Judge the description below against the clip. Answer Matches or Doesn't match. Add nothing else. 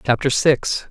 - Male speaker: Matches